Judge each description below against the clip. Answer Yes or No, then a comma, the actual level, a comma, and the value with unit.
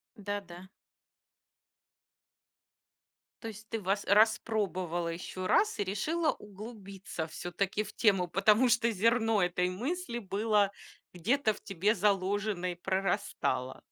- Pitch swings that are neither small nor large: Yes, average, 3.1 semitones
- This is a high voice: Yes, high, 200 Hz